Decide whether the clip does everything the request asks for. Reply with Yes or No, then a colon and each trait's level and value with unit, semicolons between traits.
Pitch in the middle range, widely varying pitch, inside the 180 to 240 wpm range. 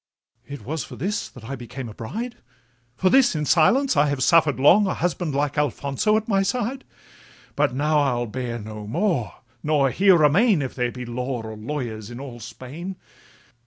Yes: medium, 145 Hz; wide, 6.7 semitones; average, 185 wpm